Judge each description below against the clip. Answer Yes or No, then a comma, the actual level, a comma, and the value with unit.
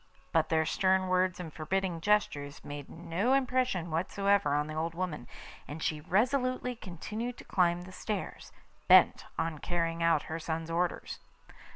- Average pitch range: Yes, average, 3.7 semitones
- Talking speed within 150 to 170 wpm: Yes, average, 155 wpm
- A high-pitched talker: No, medium, 175 Hz